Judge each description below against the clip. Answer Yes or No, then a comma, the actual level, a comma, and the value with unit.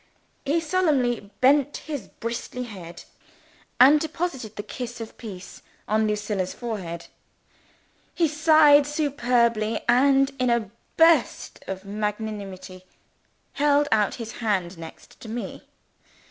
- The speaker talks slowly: Yes, slow, 115 wpm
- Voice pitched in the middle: No, high, 235 Hz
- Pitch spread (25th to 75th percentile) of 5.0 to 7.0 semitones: Yes, wide, 5.5 semitones